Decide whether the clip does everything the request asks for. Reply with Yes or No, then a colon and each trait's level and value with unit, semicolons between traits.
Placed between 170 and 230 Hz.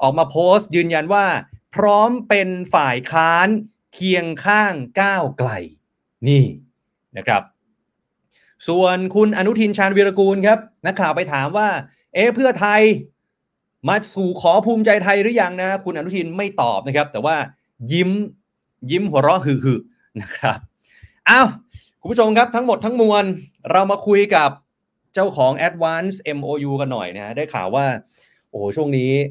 Yes: medium, 185 Hz